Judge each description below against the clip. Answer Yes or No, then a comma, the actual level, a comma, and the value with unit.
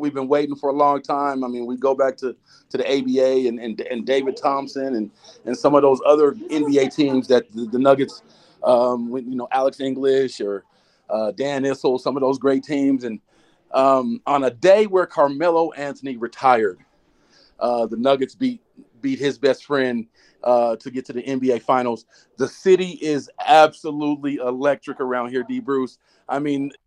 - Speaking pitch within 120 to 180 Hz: Yes, low, 135 Hz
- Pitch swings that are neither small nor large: No, narrow, 2.0 semitones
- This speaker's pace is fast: No, average, 185 wpm